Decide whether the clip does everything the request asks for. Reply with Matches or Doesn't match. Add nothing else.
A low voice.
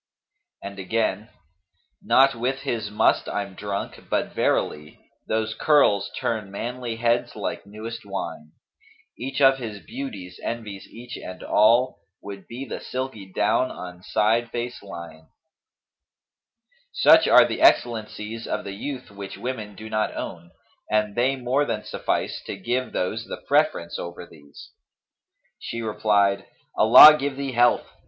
Matches